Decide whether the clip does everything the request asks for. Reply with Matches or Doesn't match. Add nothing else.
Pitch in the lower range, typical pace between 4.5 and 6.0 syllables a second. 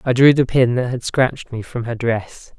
Matches